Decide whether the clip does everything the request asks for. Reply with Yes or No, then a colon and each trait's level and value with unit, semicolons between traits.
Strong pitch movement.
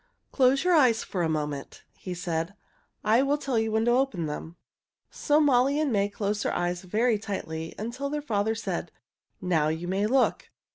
Yes: wide, 6.6 semitones